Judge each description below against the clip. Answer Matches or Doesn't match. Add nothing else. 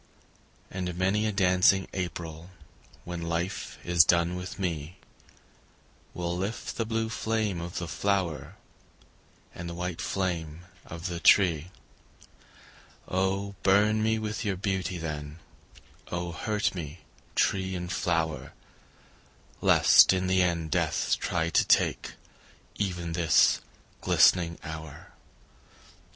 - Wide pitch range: Doesn't match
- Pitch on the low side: Matches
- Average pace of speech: Doesn't match